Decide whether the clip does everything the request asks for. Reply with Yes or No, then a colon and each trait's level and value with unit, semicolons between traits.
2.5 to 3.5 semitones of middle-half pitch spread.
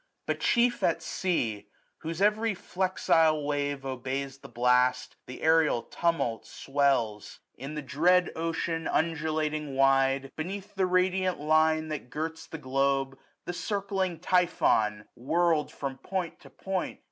No: average, 4.7 semitones